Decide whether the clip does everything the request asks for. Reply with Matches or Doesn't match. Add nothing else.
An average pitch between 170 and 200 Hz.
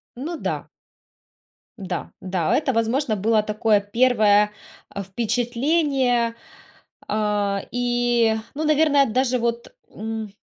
Doesn't match